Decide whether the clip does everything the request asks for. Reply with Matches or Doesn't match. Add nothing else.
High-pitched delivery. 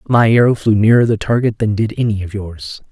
Doesn't match